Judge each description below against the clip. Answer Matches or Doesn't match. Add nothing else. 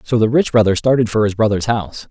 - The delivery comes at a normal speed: Doesn't match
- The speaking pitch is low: Matches